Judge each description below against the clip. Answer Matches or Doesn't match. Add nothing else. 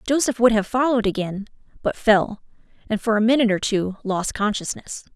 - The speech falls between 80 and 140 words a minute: Doesn't match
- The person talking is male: Doesn't match